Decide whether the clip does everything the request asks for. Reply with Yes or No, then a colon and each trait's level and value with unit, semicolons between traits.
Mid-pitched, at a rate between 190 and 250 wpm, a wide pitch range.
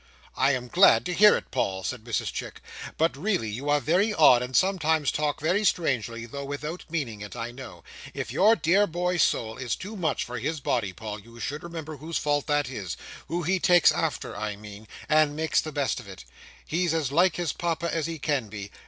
Yes: medium, 145 Hz; fast, 205 wpm; wide, 6.2 semitones